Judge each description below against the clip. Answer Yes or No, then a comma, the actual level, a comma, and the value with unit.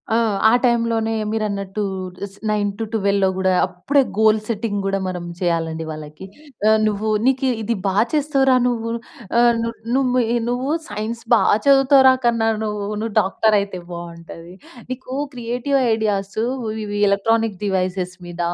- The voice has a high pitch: Yes, high, 215 Hz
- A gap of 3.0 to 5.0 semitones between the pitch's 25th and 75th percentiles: Yes, average, 3.4 semitones